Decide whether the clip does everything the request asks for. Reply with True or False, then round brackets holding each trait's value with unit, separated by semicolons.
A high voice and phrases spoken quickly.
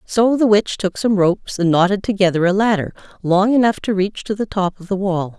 True (195 Hz; 235 wpm)